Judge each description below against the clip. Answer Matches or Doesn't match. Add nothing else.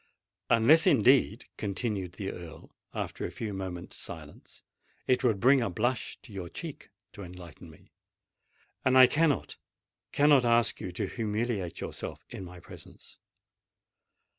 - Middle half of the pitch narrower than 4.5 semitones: Doesn't match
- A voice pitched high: Doesn't match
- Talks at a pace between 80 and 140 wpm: Matches